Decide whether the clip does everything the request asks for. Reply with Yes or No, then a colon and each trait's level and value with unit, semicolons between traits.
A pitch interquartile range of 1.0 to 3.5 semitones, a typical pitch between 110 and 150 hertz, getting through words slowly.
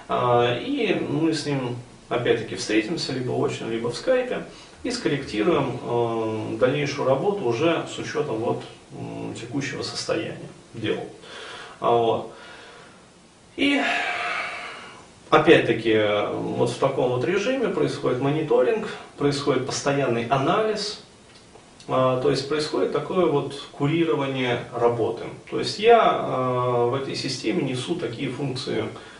No: average, 4.7 semitones; low, 135 Hz; slow, 105 wpm